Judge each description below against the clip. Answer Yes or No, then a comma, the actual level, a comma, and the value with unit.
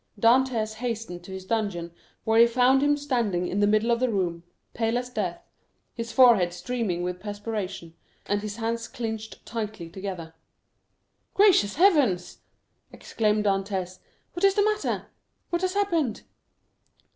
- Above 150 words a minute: No, average, 145 wpm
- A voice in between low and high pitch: No, high, 220 Hz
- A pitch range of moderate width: Yes, average, 4.6 semitones